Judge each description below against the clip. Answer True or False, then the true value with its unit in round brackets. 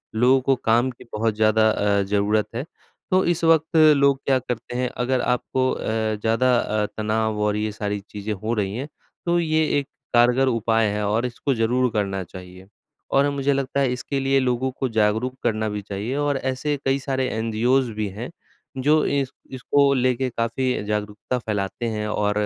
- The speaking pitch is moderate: False (120 Hz)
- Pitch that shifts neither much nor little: True (3.7 semitones)